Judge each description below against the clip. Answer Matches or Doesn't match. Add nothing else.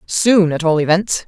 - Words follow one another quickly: Doesn't match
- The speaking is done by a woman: Matches